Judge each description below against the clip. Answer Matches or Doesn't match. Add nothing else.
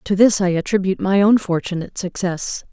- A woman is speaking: Matches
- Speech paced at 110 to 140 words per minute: Doesn't match